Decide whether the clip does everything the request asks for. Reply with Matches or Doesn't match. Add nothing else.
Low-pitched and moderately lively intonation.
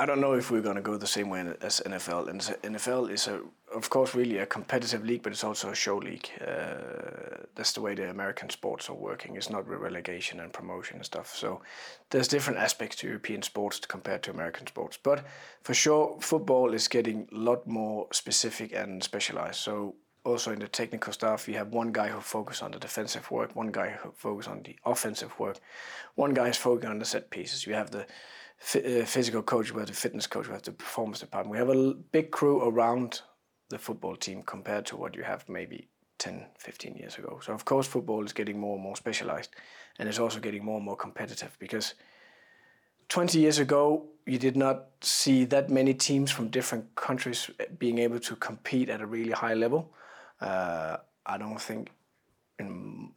Matches